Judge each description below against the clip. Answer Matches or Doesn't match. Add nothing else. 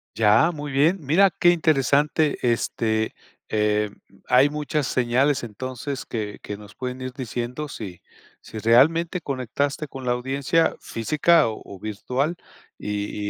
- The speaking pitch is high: Doesn't match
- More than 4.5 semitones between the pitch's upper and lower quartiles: Matches